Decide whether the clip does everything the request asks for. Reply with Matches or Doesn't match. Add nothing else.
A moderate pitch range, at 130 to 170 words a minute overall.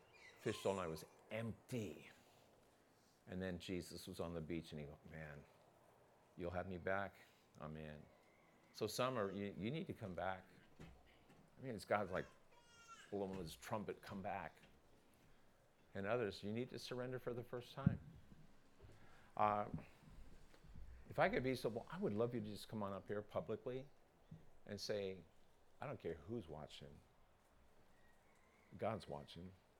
Matches